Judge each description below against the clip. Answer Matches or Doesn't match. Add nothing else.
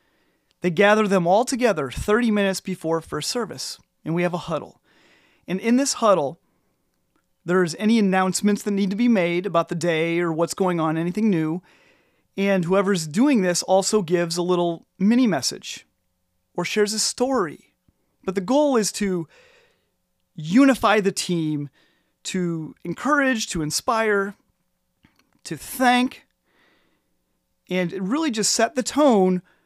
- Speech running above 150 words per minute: Doesn't match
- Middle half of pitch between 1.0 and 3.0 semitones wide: Doesn't match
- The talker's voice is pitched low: Doesn't match